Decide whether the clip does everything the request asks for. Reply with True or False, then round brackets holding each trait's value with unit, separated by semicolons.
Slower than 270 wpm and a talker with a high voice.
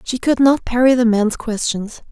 True (200 wpm; 240 Hz)